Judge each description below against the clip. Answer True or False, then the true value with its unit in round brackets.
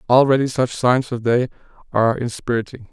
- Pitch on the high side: False (125 Hz)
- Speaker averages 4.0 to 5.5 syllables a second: False (5.7 syllables/s)